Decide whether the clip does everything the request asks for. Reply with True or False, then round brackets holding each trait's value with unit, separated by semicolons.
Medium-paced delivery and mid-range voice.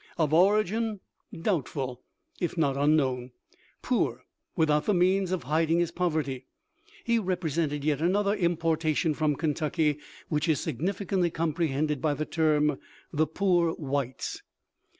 False (130 wpm; 160 Hz)